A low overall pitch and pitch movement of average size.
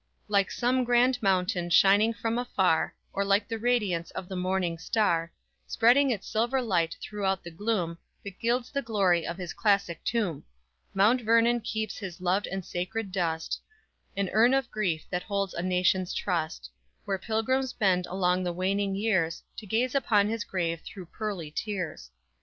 No: high, 195 Hz; average, 4.0 semitones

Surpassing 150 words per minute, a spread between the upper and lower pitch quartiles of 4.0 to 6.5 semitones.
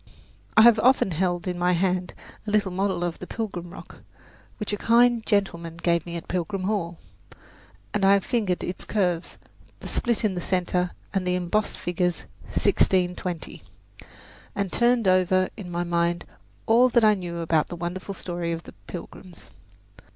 No: average, 165 wpm; average, 2.9 semitones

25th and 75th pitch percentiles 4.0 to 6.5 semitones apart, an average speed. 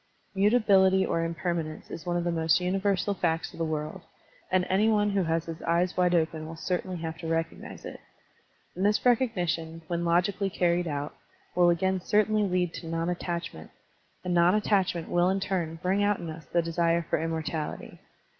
No: narrow, 2.6 semitones; average, 185 wpm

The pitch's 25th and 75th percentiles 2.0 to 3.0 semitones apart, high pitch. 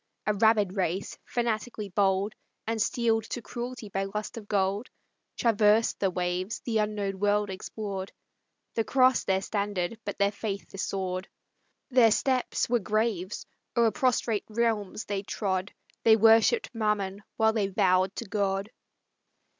Yes: narrow, 2.4 semitones; high, 210 Hz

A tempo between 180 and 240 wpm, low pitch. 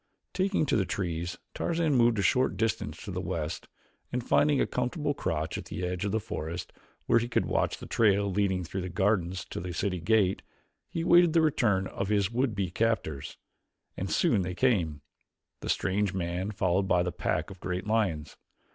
Yes: average, 190 wpm; low, 100 Hz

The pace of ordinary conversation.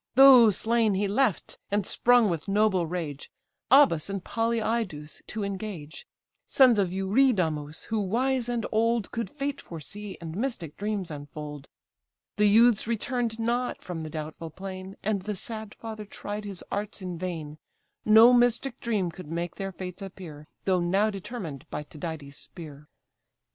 Yes: average, 150 wpm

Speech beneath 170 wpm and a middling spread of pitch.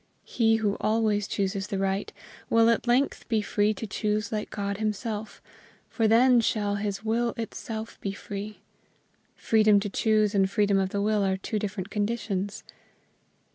No: average, 160 wpm; narrow, 1.8 semitones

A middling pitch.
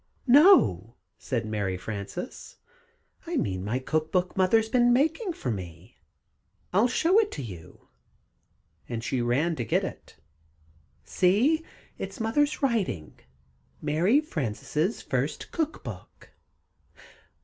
Yes: medium, 165 Hz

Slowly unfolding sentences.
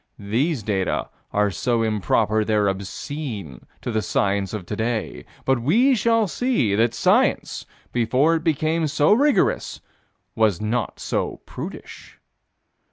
Yes: slow, 125 wpm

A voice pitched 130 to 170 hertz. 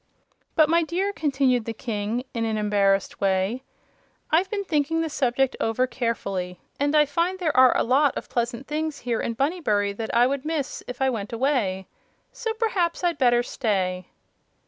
No: very high, 255 Hz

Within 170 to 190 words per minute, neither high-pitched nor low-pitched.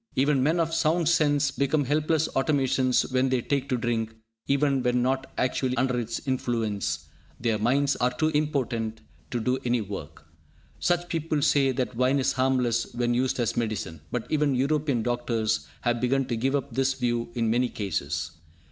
No: average, 175 wpm; low, 130 Hz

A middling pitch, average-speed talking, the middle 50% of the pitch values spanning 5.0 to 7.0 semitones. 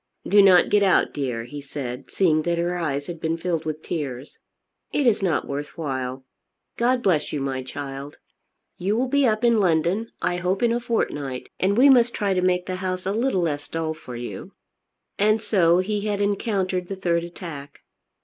Yes: medium, 180 Hz; average, 195 wpm; wide, 5.6 semitones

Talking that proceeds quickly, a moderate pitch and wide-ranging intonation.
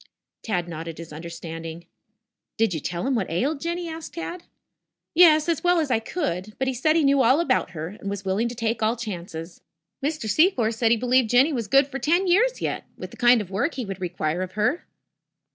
No: fast, 215 wpm; high, 230 Hz; wide, 8.5 semitones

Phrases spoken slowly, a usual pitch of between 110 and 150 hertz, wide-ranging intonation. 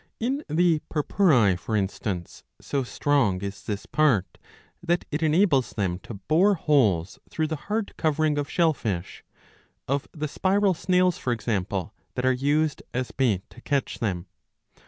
No: average, 155 wpm; medium, 140 Hz; wide, 7.6 semitones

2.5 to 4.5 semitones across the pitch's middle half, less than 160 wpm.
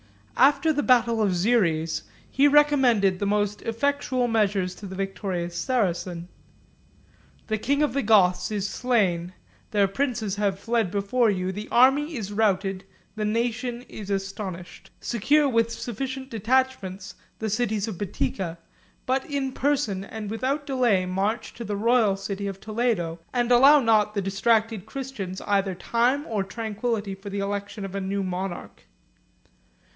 Yes: average, 4.0 semitones; average, 150 wpm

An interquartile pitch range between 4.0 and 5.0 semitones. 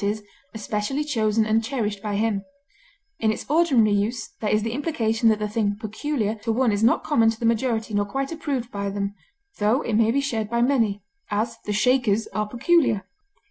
No: average, 2.9 semitones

